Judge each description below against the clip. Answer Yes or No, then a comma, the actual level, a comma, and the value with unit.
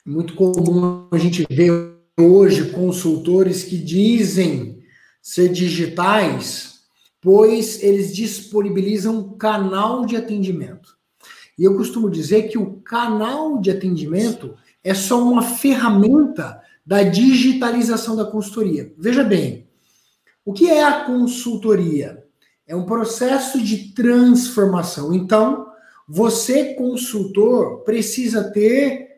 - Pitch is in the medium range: No, high, 210 Hz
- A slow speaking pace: Yes, slow, 105 wpm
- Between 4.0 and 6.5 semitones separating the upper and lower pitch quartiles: Yes, average, 4.5 semitones